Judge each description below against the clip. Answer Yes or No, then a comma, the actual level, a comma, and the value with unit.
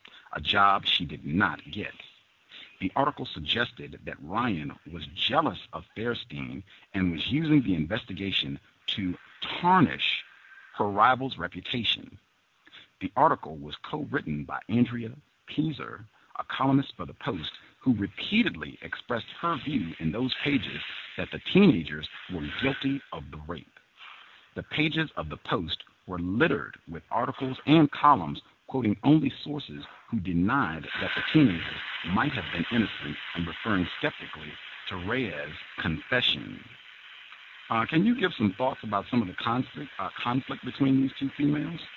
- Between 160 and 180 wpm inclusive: No, average, 145 wpm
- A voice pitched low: Yes, low, 120 Hz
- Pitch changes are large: Yes, wide, 7.3 semitones